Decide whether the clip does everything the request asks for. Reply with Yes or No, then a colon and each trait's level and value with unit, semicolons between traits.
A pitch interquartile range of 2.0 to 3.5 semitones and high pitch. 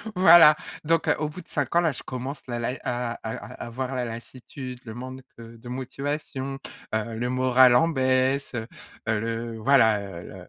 No: average, 2.9 semitones; low, 130 Hz